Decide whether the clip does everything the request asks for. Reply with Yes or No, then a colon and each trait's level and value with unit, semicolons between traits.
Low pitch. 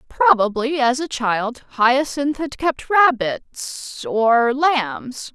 No: very high, 260 Hz